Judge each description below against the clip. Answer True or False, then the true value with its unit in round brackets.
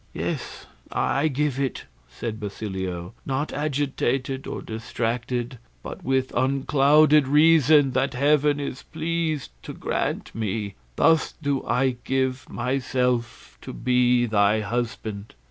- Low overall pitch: True (130 Hz)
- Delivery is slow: True (115 wpm)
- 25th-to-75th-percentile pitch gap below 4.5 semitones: True (3.5 semitones)